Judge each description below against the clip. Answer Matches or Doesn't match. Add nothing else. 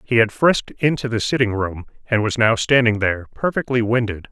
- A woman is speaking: Doesn't match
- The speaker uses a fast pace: Doesn't match